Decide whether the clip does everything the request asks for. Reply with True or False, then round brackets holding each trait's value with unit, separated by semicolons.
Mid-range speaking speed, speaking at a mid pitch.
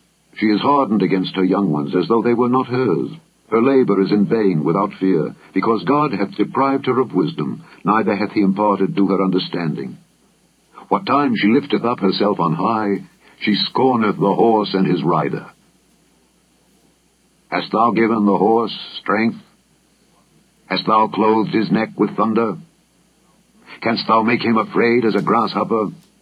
False (160 wpm; 110 Hz)